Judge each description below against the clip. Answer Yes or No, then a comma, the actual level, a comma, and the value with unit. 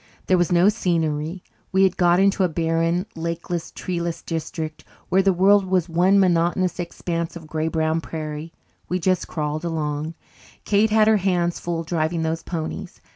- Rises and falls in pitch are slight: Yes, narrow, 2.2 semitones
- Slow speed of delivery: No, average, 165 wpm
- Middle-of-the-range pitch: Yes, medium, 170 Hz